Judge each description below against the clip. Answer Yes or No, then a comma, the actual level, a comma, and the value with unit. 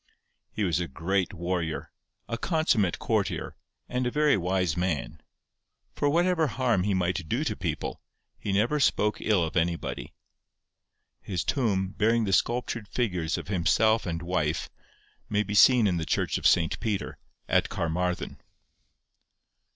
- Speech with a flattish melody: No, average, 5.1 semitones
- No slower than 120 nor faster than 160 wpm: Yes, average, 145 wpm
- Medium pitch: No, very low, 95 Hz